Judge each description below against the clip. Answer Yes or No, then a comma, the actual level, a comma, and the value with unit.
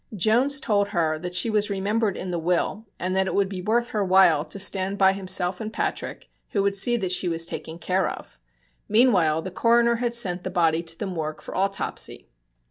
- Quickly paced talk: Yes, fast, 215 wpm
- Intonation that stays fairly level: No, average, 3.2 semitones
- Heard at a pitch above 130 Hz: Yes, high, 190 Hz